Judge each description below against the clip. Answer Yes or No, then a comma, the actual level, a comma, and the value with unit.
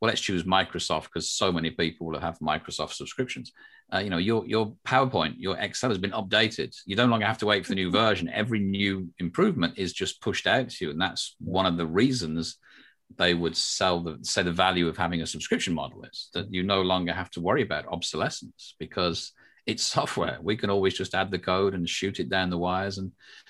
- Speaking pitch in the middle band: No, very low, 95 Hz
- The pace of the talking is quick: Yes, fast, 220 wpm